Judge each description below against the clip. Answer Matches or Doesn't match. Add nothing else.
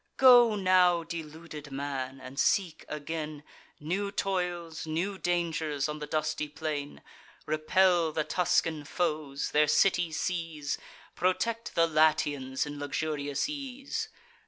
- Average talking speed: Doesn't match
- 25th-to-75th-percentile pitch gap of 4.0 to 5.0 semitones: Doesn't match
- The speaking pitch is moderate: Matches